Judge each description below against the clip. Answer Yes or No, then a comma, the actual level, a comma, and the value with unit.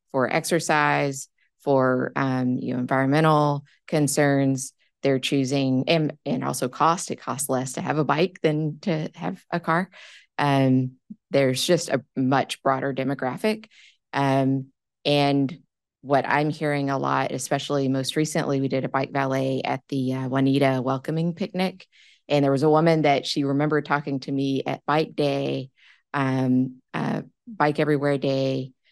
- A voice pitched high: No, medium, 140 Hz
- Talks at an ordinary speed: Yes, average, 150 wpm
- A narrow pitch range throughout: Yes, narrow, 2.3 semitones